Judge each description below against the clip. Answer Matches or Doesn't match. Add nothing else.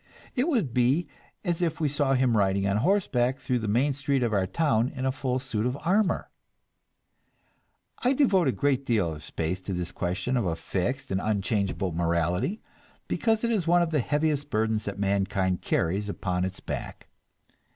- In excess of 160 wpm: Matches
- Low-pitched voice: Matches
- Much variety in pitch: Matches